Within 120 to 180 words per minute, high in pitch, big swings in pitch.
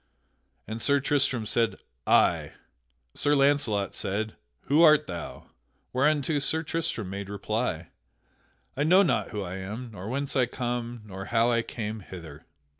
No: average, 145 wpm; low, 115 Hz; wide, 5.7 semitones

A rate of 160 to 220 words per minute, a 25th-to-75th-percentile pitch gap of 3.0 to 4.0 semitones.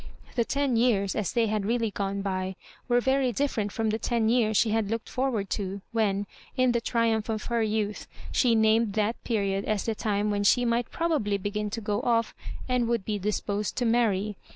No: average, 200 wpm; narrow, 2.5 semitones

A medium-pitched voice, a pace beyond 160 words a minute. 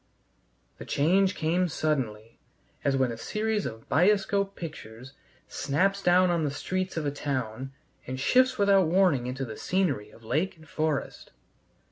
No: medium, 155 Hz; average, 150 wpm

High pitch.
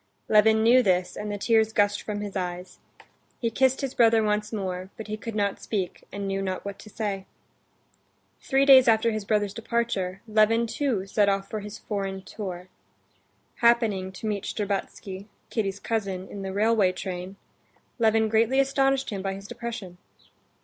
Yes: high, 210 Hz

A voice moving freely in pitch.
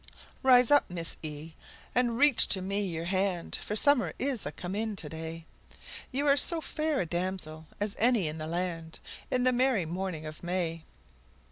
Yes: wide, 7.0 semitones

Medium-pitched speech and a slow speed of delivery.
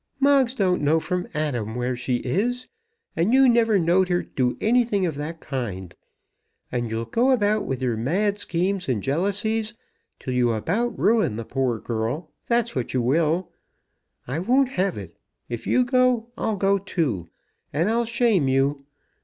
No: medium, 175 Hz; average, 165 wpm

